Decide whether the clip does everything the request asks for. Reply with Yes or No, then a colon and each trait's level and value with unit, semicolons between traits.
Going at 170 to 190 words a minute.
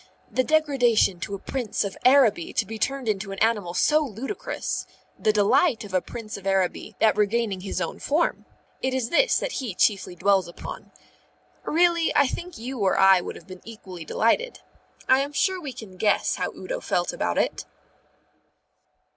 Yes: average, 180 wpm